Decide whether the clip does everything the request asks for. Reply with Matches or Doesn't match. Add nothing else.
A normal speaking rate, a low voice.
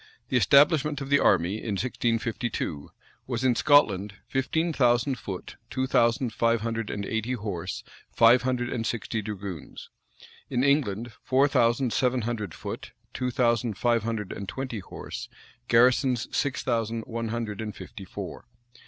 Matches